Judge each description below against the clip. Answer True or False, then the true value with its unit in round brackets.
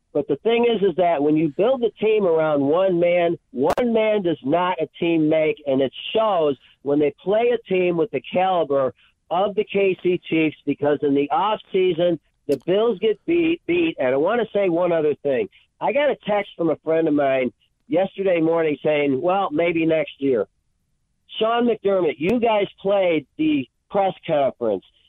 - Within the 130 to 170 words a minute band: False (185 wpm)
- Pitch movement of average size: False (5.8 semitones)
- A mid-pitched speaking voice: True (180 Hz)